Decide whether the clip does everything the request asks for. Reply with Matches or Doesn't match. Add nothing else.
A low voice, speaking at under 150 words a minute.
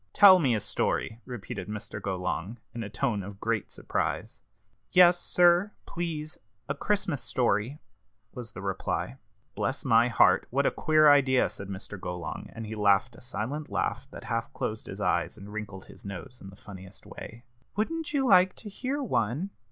Doesn't match